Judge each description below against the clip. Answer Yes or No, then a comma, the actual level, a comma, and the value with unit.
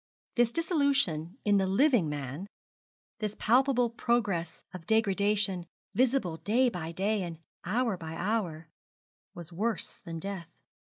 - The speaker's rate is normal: No, slow, 125 wpm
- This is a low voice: No, high, 200 Hz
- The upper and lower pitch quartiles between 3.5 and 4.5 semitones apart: No, wide, 5.6 semitones